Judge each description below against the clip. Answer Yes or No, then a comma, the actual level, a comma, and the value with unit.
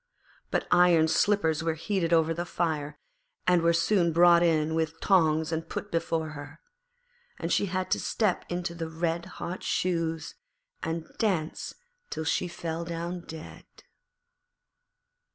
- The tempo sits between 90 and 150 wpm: Yes, average, 140 wpm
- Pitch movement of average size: No, narrow, 1.6 semitones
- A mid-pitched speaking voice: Yes, medium, 165 Hz